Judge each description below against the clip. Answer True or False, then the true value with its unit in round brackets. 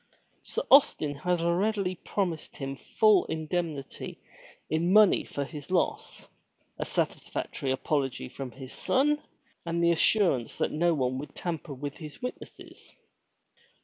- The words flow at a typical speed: False (130 wpm)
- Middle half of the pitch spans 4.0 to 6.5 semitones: True (4.6 semitones)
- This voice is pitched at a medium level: True (165 Hz)